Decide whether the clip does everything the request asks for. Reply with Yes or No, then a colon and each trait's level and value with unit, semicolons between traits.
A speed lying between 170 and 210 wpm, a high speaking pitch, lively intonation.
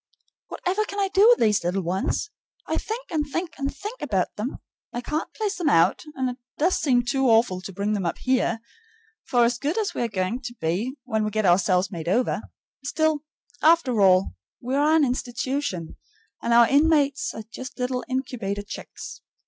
Yes: average, 190 wpm; very high, 250 Hz; wide, 6.7 semitones